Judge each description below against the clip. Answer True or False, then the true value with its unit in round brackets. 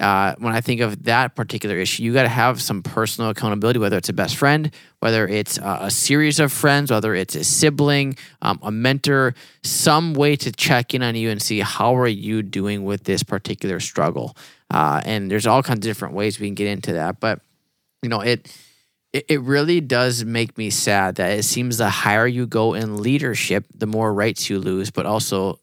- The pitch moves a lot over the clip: False (4.3 semitones)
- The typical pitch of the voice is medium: False (115 Hz)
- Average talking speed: False (215 wpm)